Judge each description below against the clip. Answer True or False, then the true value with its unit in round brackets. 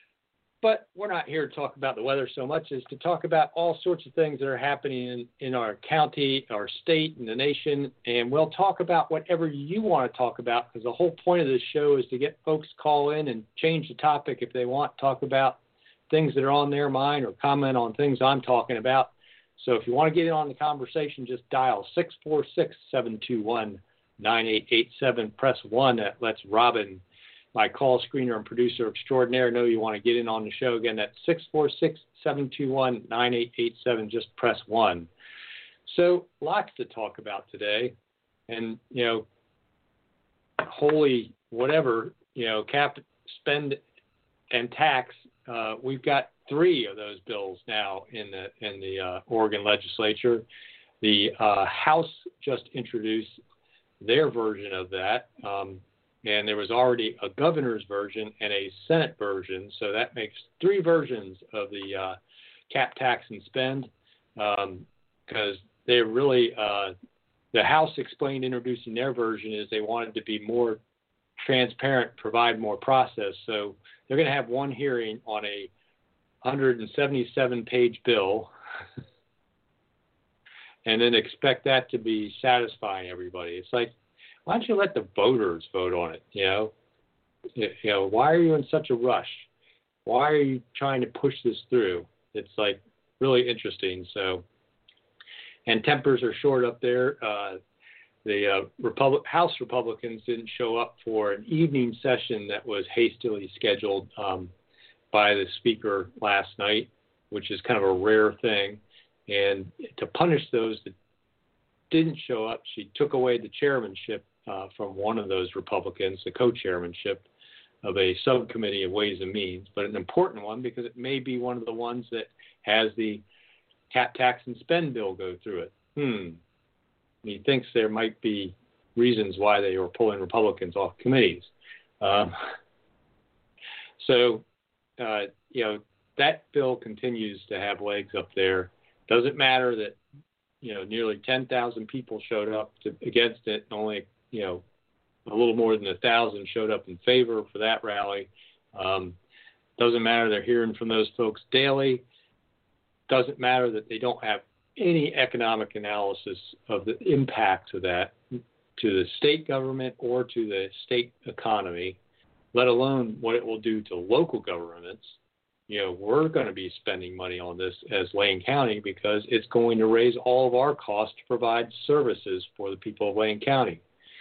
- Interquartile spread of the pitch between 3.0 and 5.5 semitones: True (4.4 semitones)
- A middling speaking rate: True (170 wpm)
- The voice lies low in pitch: True (120 Hz)